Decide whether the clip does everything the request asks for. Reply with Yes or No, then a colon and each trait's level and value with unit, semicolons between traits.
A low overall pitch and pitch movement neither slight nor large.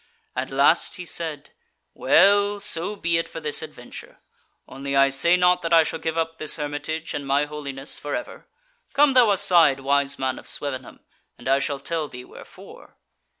No: medium, 155 Hz; average, 3.5 semitones